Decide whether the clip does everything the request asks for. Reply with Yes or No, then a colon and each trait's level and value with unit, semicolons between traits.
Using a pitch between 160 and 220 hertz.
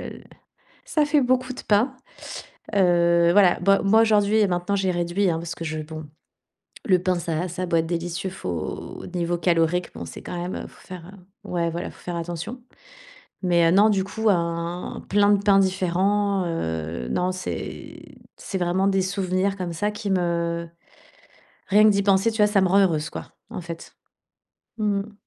Yes: medium, 185 Hz